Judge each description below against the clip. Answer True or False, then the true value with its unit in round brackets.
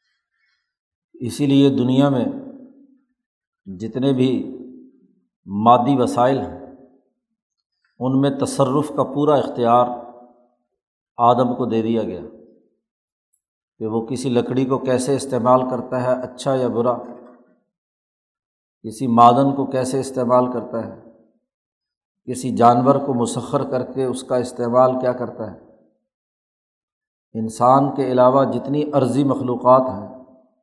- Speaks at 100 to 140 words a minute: True (115 wpm)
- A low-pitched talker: True (125 Hz)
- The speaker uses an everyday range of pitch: False (2.1 semitones)